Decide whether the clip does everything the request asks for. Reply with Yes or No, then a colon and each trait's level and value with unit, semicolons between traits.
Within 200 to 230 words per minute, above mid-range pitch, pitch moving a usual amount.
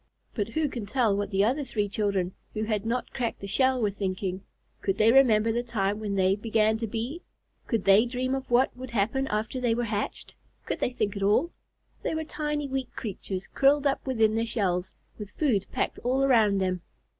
Yes: fast, 205 wpm; high, 225 Hz; average, 4.2 semitones